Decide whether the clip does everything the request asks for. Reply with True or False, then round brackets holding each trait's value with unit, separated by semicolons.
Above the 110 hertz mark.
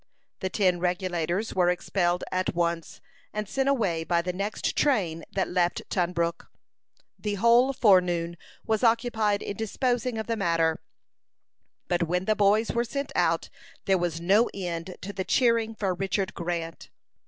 True (190 Hz)